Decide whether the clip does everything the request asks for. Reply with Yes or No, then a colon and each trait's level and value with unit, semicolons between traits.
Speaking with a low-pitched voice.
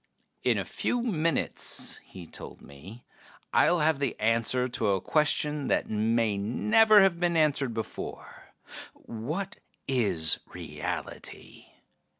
Yes: low, 130 Hz